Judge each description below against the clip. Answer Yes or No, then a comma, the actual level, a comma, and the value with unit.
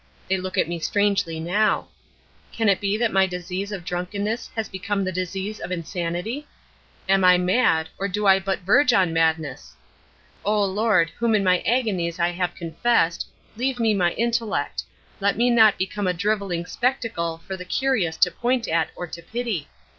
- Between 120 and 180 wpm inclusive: Yes, average, 175 wpm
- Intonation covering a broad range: No, average, 3.7 semitones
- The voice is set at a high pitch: Yes, high, 195 Hz